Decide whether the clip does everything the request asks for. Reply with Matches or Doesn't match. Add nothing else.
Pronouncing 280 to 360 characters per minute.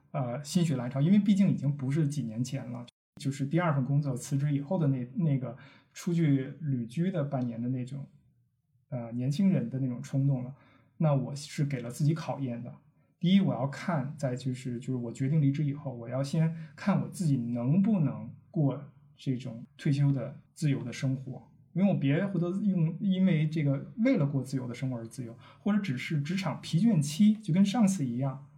Matches